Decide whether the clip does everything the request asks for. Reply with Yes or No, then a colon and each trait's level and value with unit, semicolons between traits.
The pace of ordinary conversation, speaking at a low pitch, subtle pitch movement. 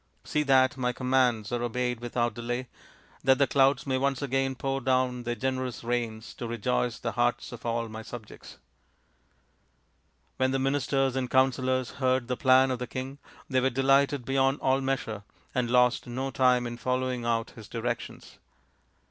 Yes: average, 165 wpm; low, 130 Hz; narrow, 1.7 semitones